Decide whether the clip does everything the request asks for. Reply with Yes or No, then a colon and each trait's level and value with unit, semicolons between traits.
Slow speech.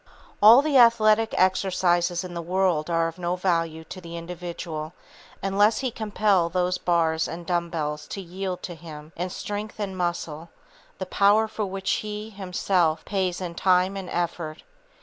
No: average, 165 wpm